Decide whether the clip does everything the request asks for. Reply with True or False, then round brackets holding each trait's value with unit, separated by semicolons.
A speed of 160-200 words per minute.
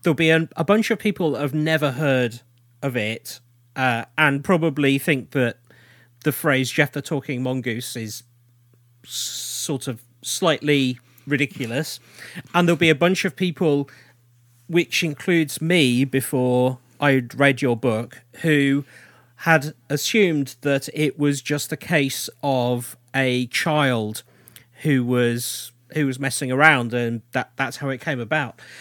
False (140 wpm)